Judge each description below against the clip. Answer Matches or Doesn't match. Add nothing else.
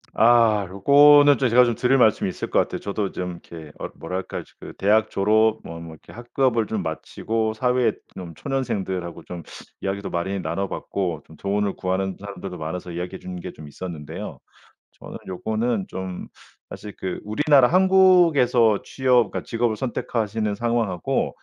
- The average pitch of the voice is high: Doesn't match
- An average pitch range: Matches